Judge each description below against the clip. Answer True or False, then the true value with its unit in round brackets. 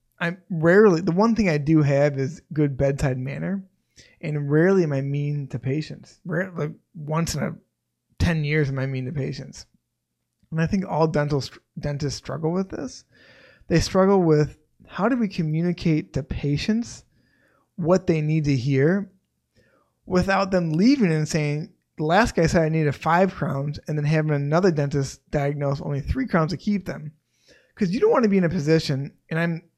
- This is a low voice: False (160 Hz)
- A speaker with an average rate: True (180 wpm)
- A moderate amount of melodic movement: True (4.0 semitones)